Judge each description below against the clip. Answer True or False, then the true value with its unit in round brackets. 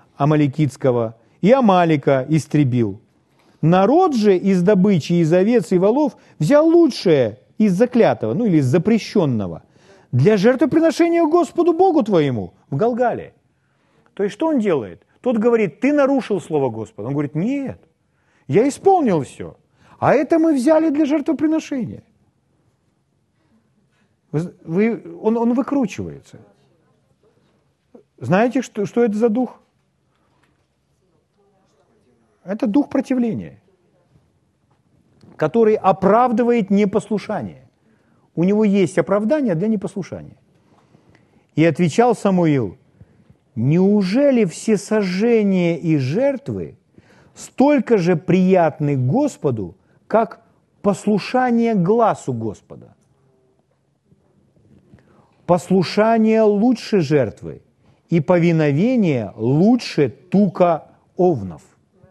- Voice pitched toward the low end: False (200 Hz)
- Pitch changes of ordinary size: False (7.5 semitones)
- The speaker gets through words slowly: True (95 wpm)